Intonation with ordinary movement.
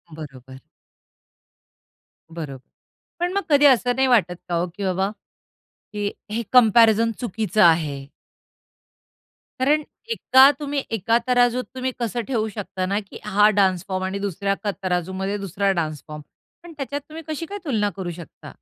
No: wide, 5.8 semitones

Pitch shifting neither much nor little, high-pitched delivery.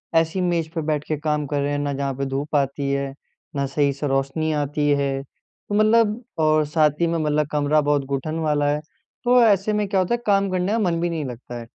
No: average, 3.6 semitones; medium, 150 Hz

